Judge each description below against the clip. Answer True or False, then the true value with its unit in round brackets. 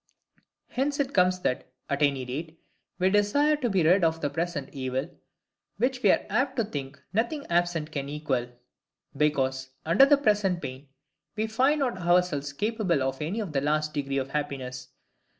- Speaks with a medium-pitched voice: True (165 Hz)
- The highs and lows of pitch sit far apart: True (7.3 semitones)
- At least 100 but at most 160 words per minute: False (170 wpm)